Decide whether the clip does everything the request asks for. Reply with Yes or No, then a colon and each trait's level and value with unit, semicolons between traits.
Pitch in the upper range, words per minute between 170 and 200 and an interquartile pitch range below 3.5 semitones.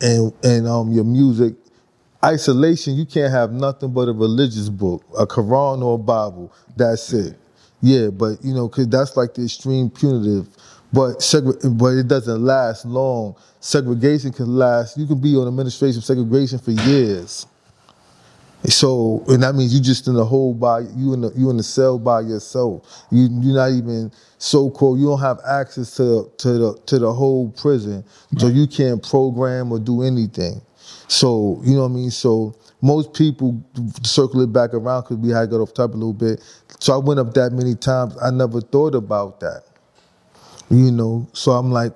No: low, 125 Hz; average, 190 wpm; narrow, 2.5 semitones